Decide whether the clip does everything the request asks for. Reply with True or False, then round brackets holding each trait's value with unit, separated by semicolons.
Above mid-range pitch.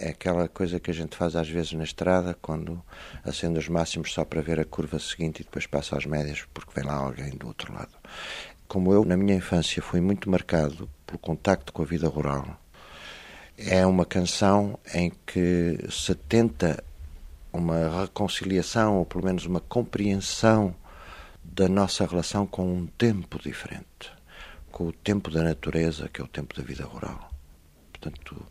False (85 Hz)